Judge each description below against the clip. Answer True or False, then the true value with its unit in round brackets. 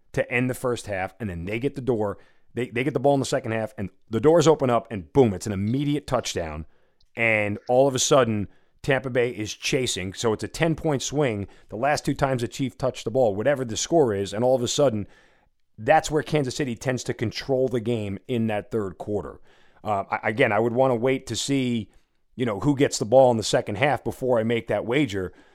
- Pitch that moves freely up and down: False (4.5 semitones)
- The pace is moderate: False (235 wpm)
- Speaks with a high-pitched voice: False (120 Hz)